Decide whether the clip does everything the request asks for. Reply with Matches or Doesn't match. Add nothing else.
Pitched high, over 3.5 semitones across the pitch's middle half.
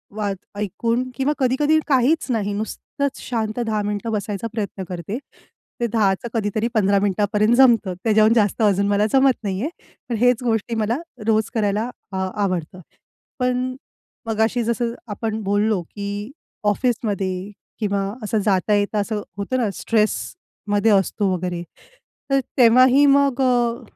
Doesn't match